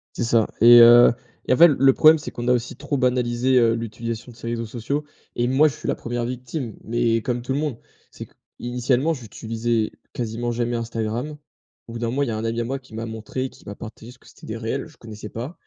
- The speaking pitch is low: Yes, low, 120 Hz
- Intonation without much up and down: Yes, narrow, 2.0 semitones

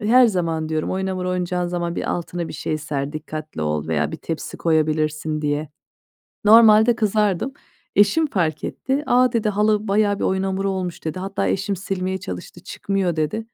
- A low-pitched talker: No, medium, 185 Hz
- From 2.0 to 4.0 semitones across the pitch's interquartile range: No, average, 4.9 semitones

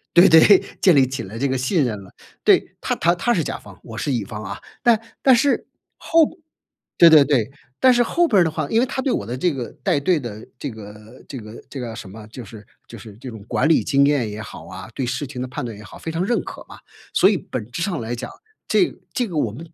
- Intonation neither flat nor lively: No, wide, 7.4 semitones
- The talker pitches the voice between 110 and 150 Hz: Yes, low, 135 Hz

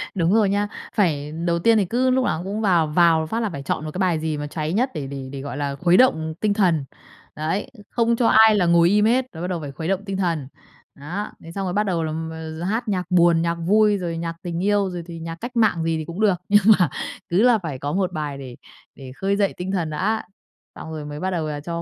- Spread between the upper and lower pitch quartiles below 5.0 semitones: Yes, average, 4.4 semitones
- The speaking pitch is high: No, medium, 175 Hz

